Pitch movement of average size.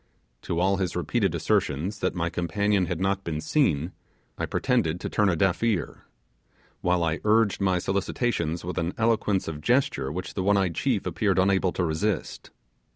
Yes: average, 3.2 semitones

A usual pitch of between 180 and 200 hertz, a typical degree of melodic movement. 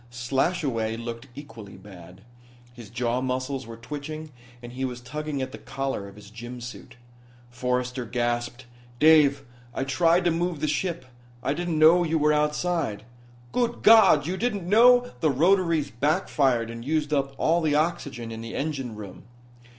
No: low, 135 Hz; average, 4.9 semitones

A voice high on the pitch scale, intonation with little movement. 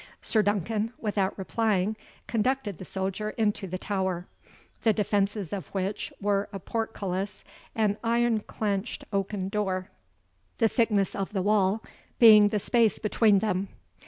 Yes: high, 205 Hz; narrow, 2.2 semitones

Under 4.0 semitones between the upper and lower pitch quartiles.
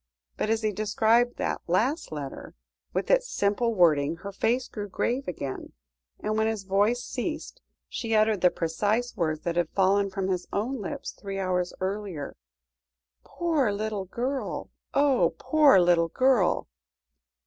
No: average, 4.9 semitones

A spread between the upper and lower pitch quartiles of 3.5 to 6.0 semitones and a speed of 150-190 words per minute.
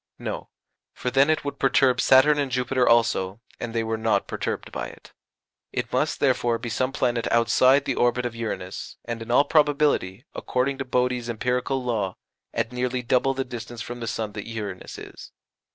No: narrow, 2.6 semitones; average, 185 wpm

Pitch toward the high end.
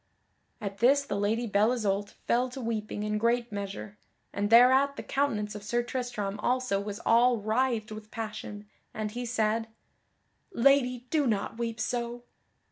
Yes: high, 225 Hz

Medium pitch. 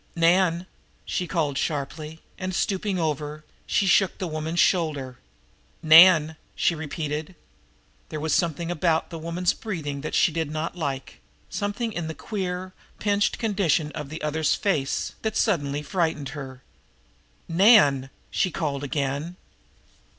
Yes: medium, 160 Hz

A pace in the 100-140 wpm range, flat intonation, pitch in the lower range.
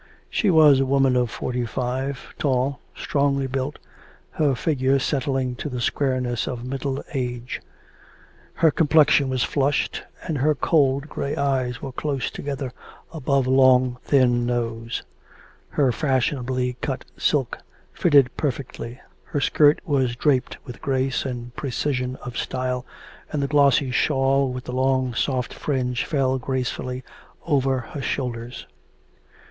Yes: slow, 135 wpm; narrow, 1.9 semitones; low, 130 Hz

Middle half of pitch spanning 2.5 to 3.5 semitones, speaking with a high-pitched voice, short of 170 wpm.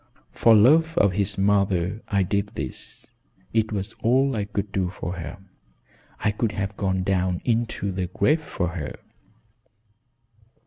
No: average, 2.9 semitones; low, 100 Hz; average, 145 wpm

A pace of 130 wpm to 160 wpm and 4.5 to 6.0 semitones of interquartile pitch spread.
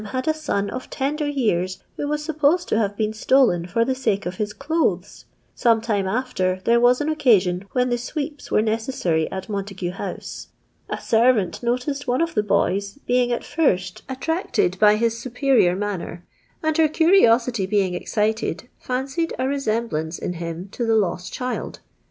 No: average, 170 wpm; wide, 5.5 semitones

